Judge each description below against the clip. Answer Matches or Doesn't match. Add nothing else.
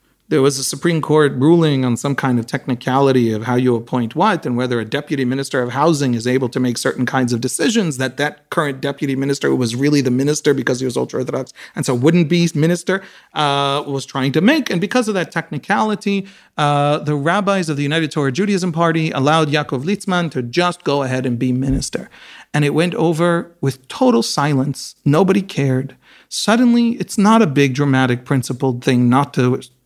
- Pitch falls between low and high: Matches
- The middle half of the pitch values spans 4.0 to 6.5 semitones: Matches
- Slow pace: Doesn't match